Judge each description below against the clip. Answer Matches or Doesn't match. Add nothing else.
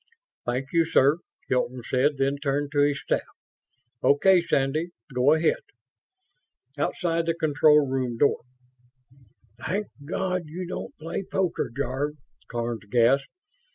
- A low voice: Doesn't match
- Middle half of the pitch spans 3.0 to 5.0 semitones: Matches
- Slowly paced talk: Matches